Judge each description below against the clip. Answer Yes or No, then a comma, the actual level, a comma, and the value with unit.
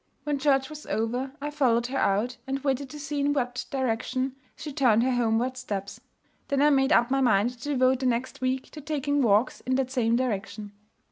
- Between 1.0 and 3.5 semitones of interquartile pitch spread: Yes, average, 2.7 semitones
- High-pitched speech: Yes, very high, 260 Hz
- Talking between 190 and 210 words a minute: Yes, fast, 205 wpm